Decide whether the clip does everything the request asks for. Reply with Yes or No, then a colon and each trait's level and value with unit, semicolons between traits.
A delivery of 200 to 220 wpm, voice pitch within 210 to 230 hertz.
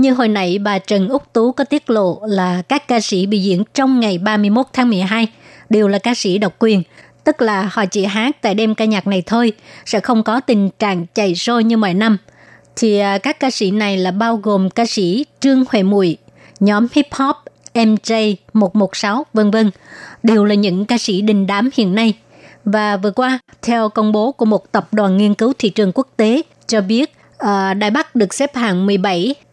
Yes: average, 205 wpm; high, 215 Hz